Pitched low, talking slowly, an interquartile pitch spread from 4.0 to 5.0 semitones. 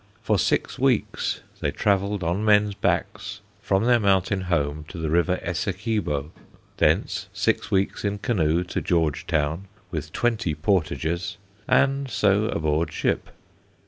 Yes: very low, 95 Hz; slow, 130 wpm; average, 4.3 semitones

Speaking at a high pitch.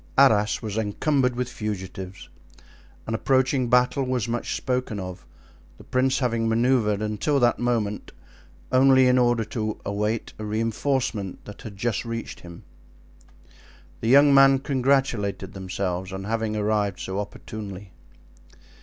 No: low, 115 Hz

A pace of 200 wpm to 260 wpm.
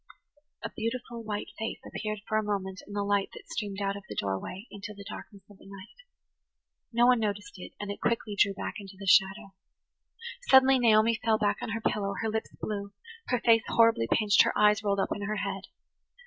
Yes: fast, 205 wpm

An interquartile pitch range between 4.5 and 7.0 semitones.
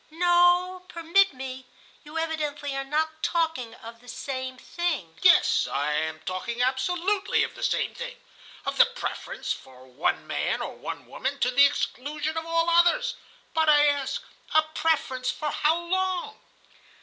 Yes: average, 5.0 semitones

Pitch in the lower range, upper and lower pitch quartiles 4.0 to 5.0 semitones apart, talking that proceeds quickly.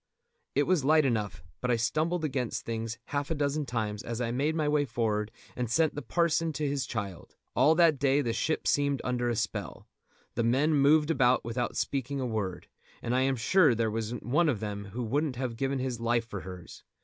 Yes: low, 125 Hz; average, 4.3 semitones; fast, 210 wpm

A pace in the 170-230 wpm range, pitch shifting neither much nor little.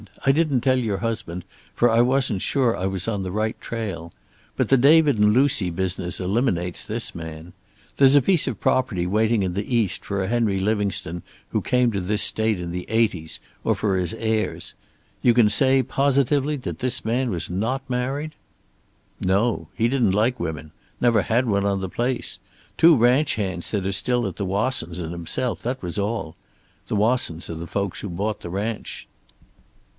Yes: average, 185 wpm; average, 4.9 semitones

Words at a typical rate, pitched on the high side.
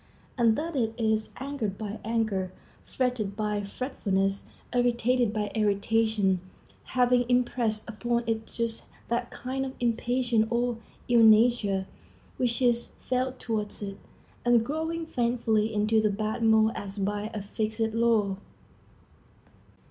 No: slow, 125 wpm; high, 225 Hz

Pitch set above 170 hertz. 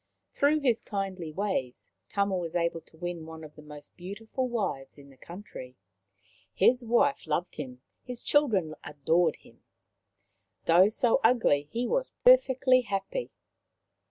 Yes: high, 190 Hz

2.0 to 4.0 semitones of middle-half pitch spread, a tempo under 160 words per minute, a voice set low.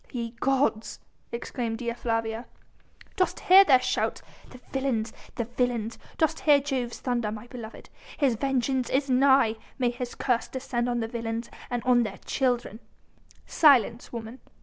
No: narrow, 2.5 semitones; average, 150 wpm; high, 245 Hz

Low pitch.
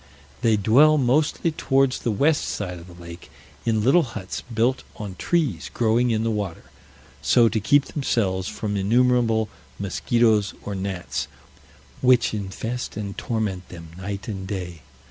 Yes: low, 110 Hz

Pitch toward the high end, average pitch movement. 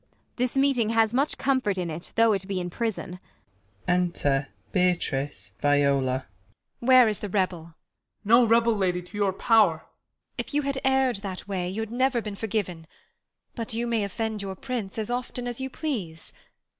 Yes: high, 210 Hz; average, 4.9 semitones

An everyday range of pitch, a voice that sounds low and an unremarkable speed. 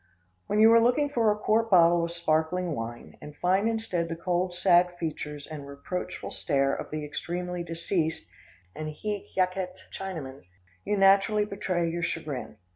No: average, 3.7 semitones; medium, 175 Hz; average, 160 wpm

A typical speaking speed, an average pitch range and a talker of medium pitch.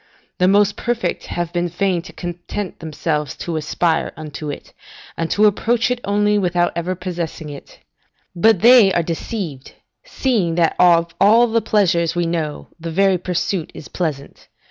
Yes: average, 160 wpm; average, 3.6 semitones; medium, 175 Hz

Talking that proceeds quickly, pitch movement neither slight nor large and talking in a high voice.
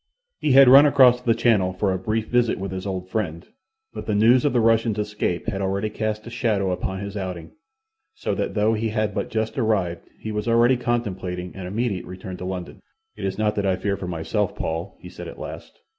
No: fast, 220 wpm; average, 3.4 semitones; low, 105 Hz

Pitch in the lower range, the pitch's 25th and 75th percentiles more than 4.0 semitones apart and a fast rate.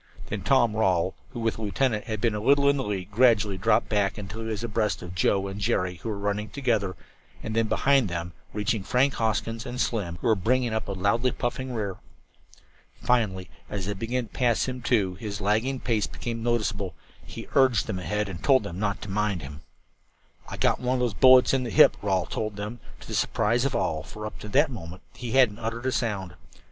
No: low, 110 Hz; average, 3.5 semitones; fast, 220 wpm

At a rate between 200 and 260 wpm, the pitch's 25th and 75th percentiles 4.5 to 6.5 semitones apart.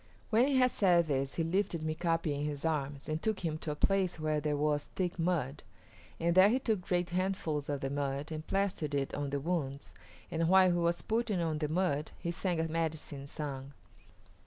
No: fast, 205 wpm; average, 3.6 semitones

